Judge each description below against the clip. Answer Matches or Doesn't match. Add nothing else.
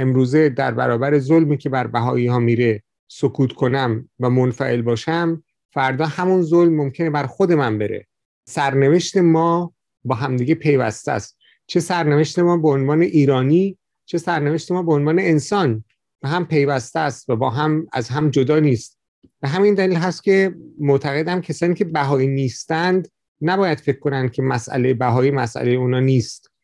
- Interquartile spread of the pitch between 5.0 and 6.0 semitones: Doesn't match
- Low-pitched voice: Doesn't match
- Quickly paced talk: Matches